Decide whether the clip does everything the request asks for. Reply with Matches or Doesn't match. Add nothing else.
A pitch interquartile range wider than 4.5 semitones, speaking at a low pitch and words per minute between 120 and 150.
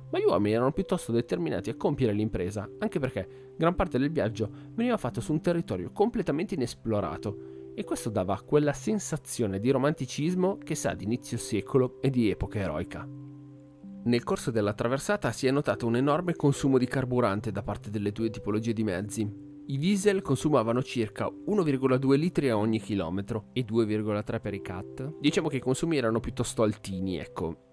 Doesn't match